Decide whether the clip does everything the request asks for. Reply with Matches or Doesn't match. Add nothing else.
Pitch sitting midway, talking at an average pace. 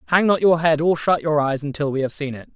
Doesn't match